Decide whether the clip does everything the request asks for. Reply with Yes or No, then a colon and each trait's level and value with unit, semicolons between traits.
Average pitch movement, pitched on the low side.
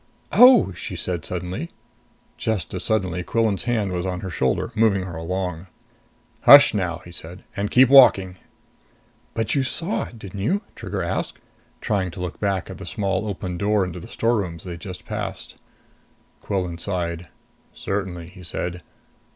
Yes: average, 3.4 semitones; very low, 95 Hz